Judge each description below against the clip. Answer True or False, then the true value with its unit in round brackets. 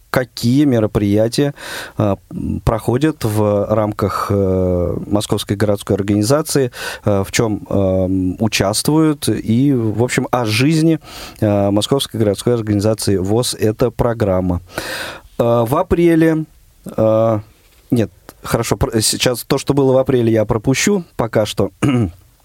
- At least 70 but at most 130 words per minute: True (120 wpm)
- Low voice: True (110 Hz)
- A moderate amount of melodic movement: True (4.4 semitones)